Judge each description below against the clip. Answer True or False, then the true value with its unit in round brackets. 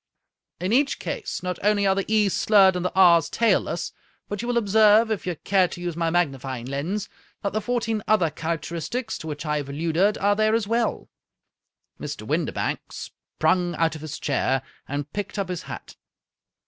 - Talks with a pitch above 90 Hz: True (185 Hz)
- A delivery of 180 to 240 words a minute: True (185 wpm)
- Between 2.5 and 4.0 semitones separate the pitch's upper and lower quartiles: False (4.5 semitones)